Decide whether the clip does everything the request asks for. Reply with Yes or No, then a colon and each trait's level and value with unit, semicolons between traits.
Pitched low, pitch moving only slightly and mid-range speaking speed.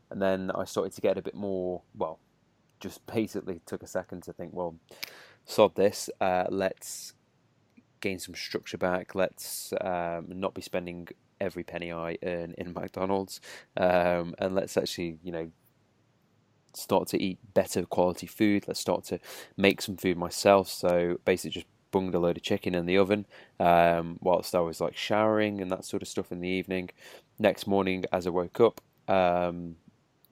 Yes: very low, 90 Hz; narrow, 1.8 semitones; average, 175 wpm